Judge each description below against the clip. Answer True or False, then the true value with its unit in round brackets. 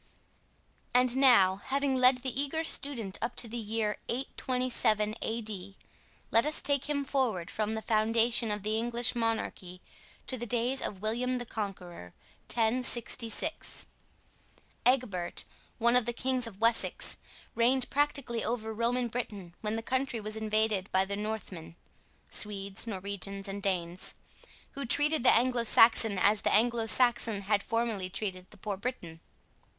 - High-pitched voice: True (225 Hz)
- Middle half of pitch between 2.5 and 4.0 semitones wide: True (3.6 semitones)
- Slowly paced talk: False (145 wpm)